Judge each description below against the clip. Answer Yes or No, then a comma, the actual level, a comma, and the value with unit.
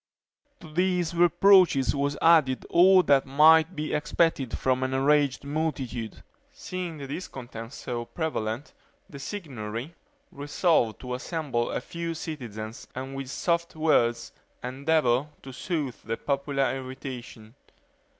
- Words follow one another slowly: Yes, slow, 120 wpm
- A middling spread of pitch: Yes, average, 4.3 semitones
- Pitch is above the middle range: No, medium, 140 Hz